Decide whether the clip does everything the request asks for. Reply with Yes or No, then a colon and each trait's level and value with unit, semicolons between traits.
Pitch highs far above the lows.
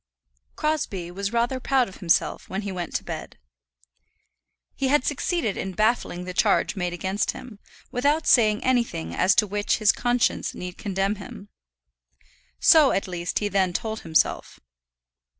No: average, 4.8 semitones